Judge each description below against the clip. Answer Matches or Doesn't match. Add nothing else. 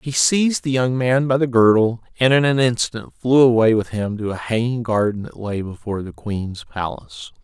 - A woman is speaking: Doesn't match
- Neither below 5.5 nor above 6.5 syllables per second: Doesn't match